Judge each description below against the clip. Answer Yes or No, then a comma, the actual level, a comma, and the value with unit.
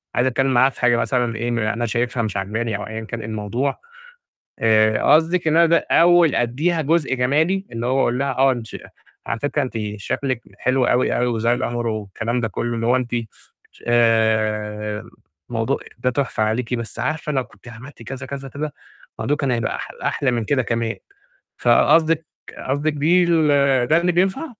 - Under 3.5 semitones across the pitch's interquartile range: No, average, 3.8 semitones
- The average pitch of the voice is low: Yes, low, 125 Hz